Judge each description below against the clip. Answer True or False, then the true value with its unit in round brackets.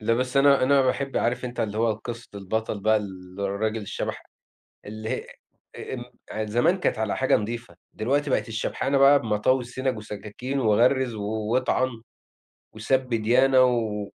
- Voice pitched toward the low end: True (115 Hz)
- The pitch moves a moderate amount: True (3.3 semitones)